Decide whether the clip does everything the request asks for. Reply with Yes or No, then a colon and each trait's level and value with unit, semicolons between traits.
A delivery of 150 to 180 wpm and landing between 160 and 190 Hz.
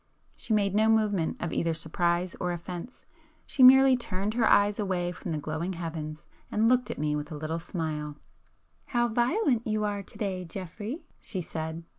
Yes: average, 175 wpm; medium, 185 Hz